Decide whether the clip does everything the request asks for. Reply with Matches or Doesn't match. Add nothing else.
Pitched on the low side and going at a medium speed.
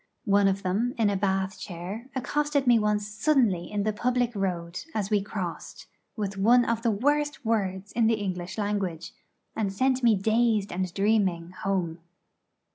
Doesn't match